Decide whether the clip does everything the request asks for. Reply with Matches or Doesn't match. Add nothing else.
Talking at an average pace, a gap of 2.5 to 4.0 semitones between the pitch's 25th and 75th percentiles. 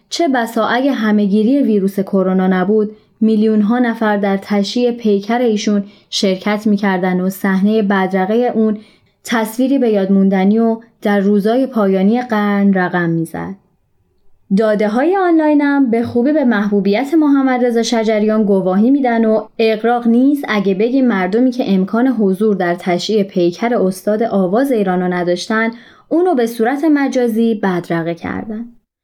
Matches